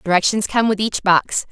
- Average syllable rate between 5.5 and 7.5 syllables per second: No, 5.0 syllables/s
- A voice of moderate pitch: No, high, 200 Hz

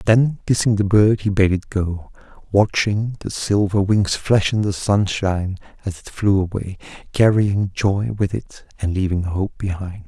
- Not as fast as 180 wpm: Yes, average, 165 wpm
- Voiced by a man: Yes, male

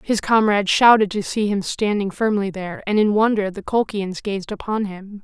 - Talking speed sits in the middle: Yes, average, 195 wpm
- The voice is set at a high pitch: Yes, high, 205 Hz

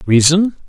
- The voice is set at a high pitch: No, medium, 165 Hz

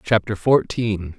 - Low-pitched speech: Yes, low, 105 Hz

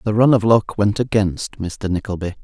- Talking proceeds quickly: No, average, 195 wpm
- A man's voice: Yes, male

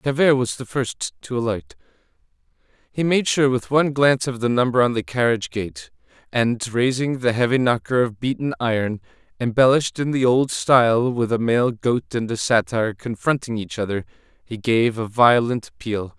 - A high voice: No, low, 120 Hz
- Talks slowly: No, average, 175 wpm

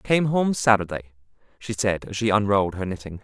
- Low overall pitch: Yes, low, 105 Hz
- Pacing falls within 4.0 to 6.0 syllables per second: No, 6.3 syllables/s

